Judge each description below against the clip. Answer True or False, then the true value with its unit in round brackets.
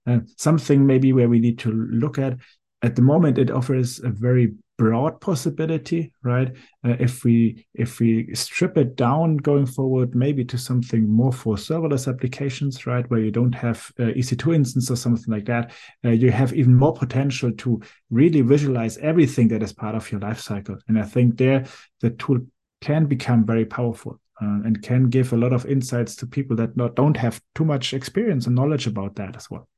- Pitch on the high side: False (125 Hz)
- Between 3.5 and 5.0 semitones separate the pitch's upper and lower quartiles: False (2.8 semitones)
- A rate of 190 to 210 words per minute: True (200 wpm)